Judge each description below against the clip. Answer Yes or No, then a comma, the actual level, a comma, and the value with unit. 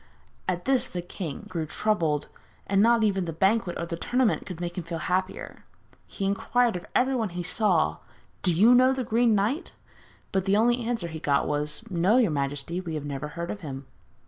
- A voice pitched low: No, medium, 185 Hz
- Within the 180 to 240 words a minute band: Yes, average, 200 wpm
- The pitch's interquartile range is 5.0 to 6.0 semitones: Yes, wide, 5.4 semitones